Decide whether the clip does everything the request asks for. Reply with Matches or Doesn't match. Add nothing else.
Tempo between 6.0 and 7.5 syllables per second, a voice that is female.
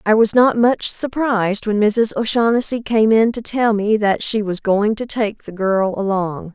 Doesn't match